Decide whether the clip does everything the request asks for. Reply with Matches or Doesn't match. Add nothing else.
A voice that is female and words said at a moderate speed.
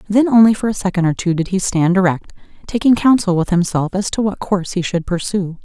Doesn't match